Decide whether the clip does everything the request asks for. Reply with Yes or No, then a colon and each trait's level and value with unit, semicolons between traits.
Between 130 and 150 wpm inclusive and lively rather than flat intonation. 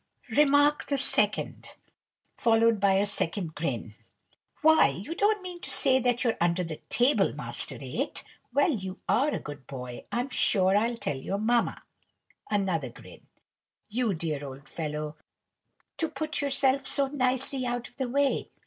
No: average, 160 wpm; wide, 8.6 semitones